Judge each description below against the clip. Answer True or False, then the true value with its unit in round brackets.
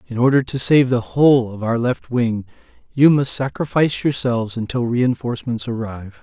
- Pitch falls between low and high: False (125 Hz)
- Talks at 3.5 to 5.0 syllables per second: False (5.3 syllables/s)